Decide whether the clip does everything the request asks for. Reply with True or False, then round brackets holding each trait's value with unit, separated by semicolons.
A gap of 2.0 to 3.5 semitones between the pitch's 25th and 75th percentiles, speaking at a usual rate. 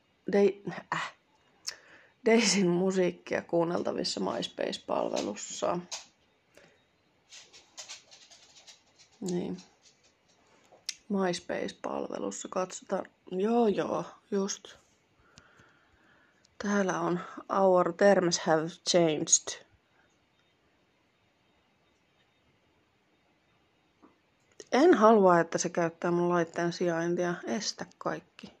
False (2.6 semitones; 60 wpm)